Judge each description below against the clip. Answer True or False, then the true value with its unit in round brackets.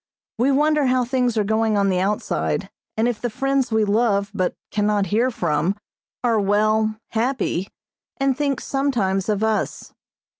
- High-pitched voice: True (220 Hz)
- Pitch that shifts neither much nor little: True (3.7 semitones)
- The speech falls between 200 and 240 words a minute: False (155 wpm)